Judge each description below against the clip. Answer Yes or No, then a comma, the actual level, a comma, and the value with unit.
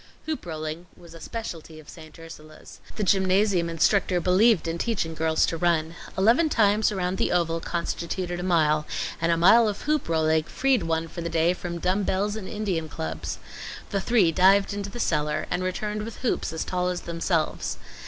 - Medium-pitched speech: Yes, medium, 175 Hz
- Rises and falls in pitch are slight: No, average, 3.7 semitones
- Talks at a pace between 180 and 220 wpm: Yes, average, 185 wpm